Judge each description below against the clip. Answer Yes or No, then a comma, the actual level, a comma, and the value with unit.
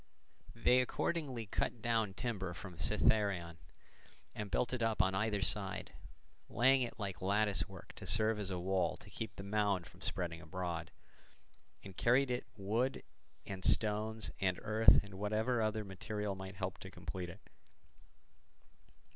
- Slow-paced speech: No, average, 155 wpm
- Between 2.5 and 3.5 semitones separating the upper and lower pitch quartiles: Yes, average, 3.0 semitones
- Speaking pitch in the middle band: No, low, 105 Hz